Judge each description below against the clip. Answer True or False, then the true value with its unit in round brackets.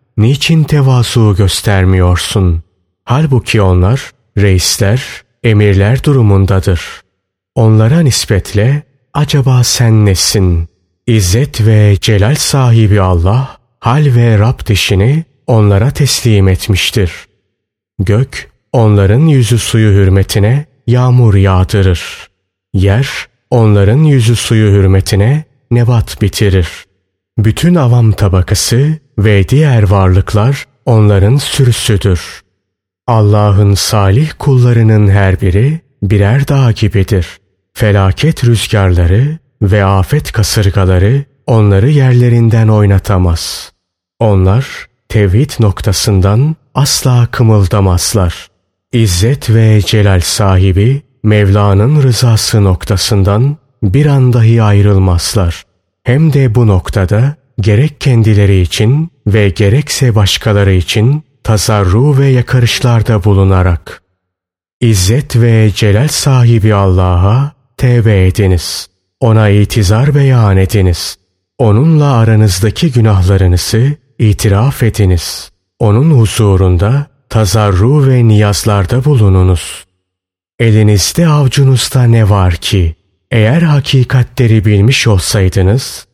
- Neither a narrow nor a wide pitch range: True (4.5 semitones)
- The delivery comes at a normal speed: False (85 wpm)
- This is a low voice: True (110 Hz)